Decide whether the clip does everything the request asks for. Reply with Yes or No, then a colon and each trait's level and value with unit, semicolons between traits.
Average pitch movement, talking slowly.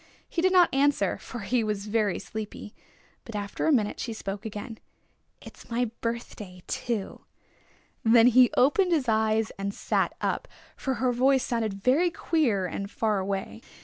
No: average, 3.7 semitones; average, 160 wpm